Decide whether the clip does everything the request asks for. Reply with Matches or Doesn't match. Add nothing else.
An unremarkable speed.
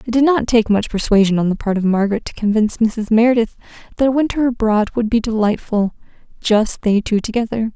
Matches